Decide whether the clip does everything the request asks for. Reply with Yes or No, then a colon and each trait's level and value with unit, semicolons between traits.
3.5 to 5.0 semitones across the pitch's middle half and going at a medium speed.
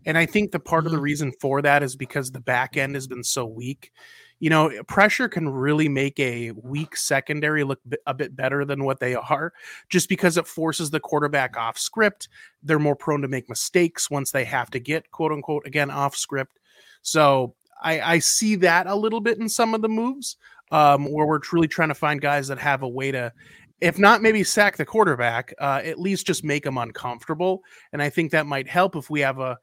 No: average, 3.9 semitones; fast, 220 wpm